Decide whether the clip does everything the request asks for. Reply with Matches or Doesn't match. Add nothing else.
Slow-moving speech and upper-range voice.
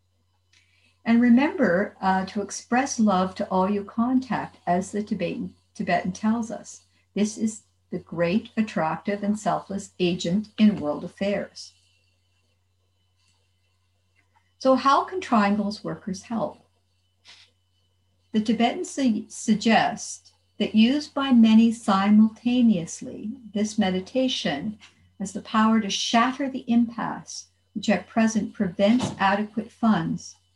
Matches